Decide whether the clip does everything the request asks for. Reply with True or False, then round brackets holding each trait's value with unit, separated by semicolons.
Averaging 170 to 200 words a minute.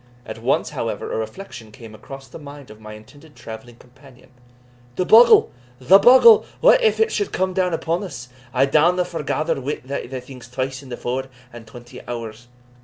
True (180 wpm)